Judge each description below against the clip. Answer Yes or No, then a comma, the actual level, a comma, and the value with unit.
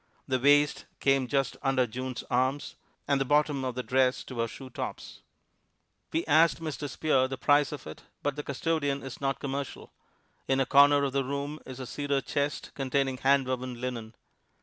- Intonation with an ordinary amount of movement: No, narrow, 1.9 semitones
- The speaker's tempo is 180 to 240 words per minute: Yes, average, 185 wpm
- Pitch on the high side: No, low, 135 Hz